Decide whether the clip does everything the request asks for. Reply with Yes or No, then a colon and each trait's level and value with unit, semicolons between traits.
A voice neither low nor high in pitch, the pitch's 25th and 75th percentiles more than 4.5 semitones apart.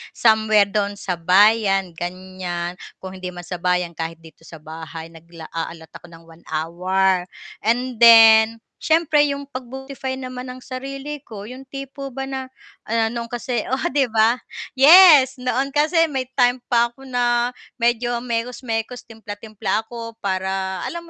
No: high, 225 Hz; wide, 5.6 semitones